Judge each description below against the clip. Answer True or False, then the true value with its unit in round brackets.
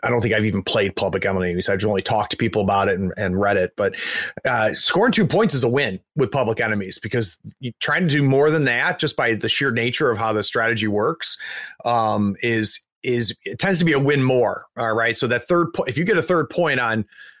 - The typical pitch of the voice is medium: False (115 Hz)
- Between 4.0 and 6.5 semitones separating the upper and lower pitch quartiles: True (4.3 semitones)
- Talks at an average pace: False (245 wpm)